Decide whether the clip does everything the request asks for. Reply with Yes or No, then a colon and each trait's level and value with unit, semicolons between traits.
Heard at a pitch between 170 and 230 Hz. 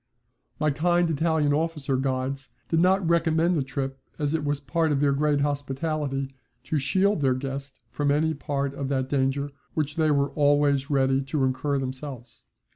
No: medium, 145 Hz